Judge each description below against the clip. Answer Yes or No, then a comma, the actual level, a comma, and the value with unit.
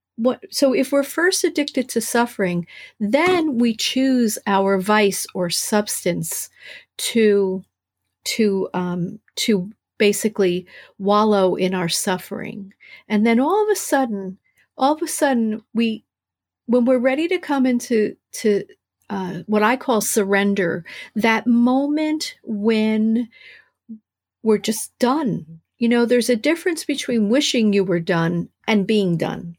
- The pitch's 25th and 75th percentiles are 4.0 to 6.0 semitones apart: Yes, average, 4.7 semitones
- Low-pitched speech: No, high, 220 Hz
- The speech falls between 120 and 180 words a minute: Yes, slow, 135 wpm